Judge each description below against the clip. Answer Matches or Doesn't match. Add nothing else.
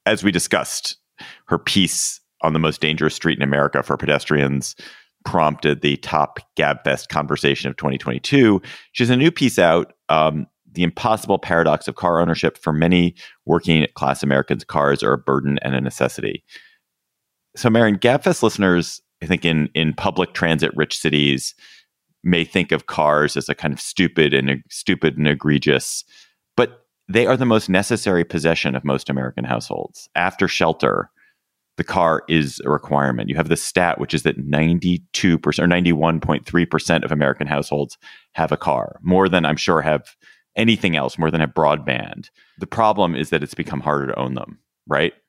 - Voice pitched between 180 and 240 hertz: Doesn't match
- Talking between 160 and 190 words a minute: Matches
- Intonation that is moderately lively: Matches